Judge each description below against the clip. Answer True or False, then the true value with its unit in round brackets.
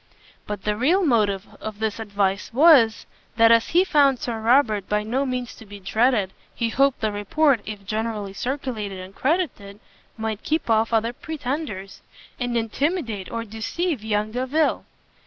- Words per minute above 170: False (155 wpm)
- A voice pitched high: True (225 Hz)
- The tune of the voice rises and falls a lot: False (4.3 semitones)